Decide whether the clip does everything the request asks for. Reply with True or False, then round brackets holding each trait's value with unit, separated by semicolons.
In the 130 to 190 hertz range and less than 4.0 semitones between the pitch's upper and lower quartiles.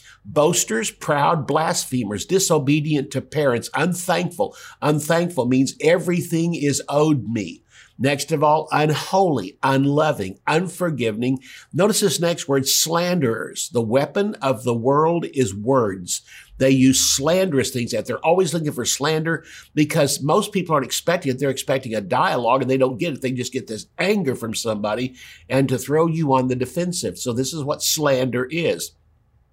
False (140 Hz; 4.3 semitones)